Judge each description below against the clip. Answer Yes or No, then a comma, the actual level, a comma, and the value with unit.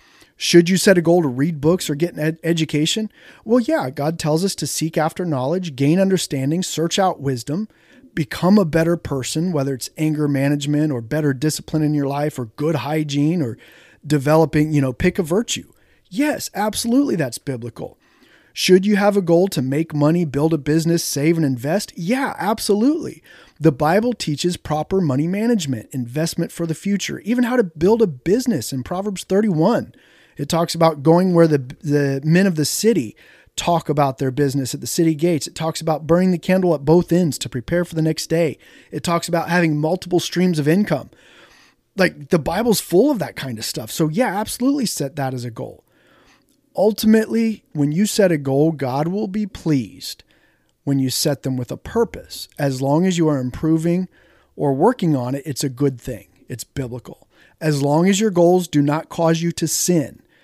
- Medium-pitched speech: Yes, medium, 160 Hz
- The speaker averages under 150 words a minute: No, average, 190 wpm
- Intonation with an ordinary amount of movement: Yes, average, 4.1 semitones